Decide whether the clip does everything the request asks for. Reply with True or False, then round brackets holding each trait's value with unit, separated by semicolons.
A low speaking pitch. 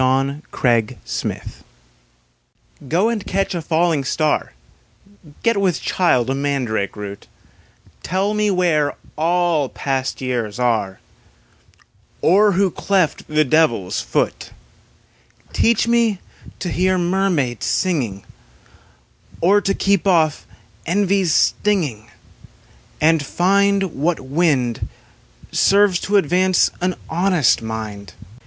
False (160 Hz)